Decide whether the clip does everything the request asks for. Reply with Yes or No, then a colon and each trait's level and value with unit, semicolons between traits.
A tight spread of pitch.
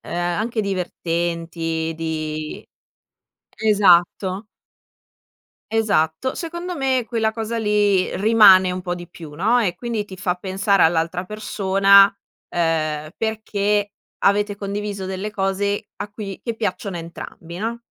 No: average, 3.5 semitones